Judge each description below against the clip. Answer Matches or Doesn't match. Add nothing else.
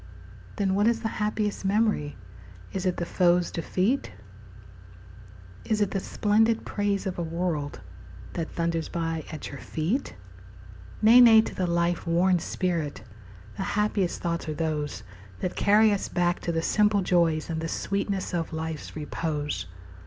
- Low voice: Doesn't match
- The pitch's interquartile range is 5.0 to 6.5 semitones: Doesn't match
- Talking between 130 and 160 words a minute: Matches